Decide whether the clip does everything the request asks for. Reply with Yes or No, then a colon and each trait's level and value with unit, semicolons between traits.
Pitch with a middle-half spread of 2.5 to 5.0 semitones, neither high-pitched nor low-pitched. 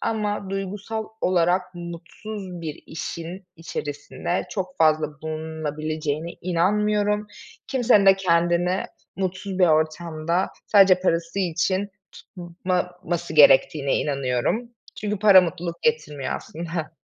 Yes: average, 3.5 semitones; medium, 175 Hz